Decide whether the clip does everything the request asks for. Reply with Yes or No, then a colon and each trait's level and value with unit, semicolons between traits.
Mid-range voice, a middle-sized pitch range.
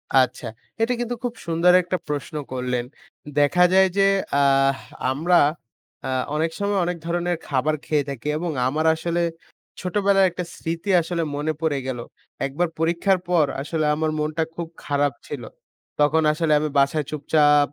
Yes: medium, 160 Hz; average, 3.3 semitones